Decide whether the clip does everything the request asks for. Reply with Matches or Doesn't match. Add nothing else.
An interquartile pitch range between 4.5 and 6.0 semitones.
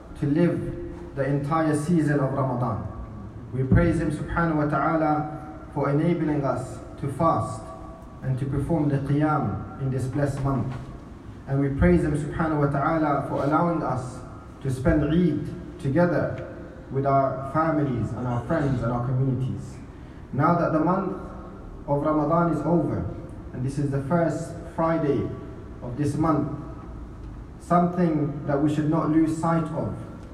Doesn't match